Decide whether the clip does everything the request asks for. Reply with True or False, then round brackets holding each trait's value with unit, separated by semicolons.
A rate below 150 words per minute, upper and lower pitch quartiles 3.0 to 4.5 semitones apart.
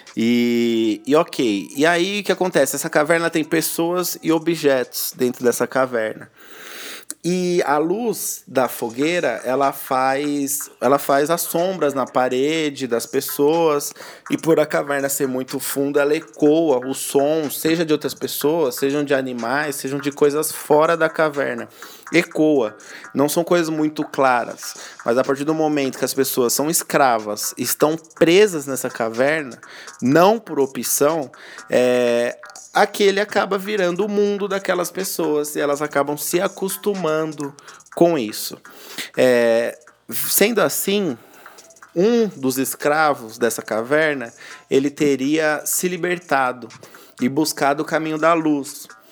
True (135 wpm; 3.8 semitones)